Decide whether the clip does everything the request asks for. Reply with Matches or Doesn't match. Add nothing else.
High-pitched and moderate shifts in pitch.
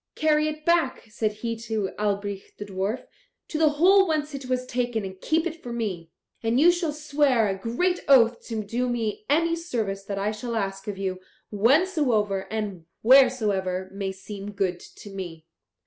Doesn't match